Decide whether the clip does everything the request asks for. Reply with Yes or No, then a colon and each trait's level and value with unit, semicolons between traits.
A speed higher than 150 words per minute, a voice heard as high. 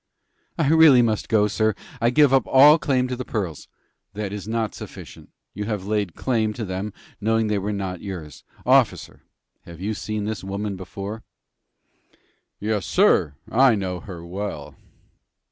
No: average, 165 wpm; low, 105 Hz